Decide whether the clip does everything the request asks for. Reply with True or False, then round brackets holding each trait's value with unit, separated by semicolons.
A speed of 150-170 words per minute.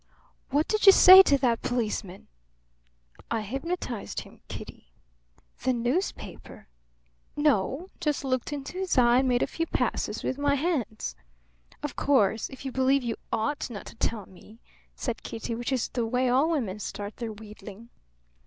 True (165 wpm)